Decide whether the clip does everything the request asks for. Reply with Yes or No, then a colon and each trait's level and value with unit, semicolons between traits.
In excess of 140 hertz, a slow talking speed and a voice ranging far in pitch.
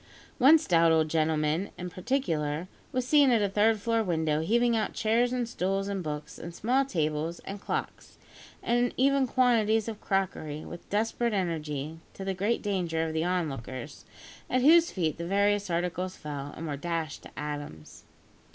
No: medium, 185 Hz; average, 170 wpm; wide, 6.1 semitones